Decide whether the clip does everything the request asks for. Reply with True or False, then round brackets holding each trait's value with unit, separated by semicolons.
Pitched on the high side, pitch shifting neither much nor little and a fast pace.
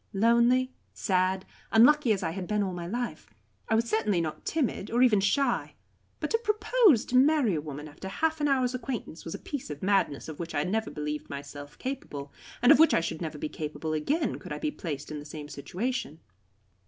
False (200 Hz; 8.5 semitones; 210 wpm)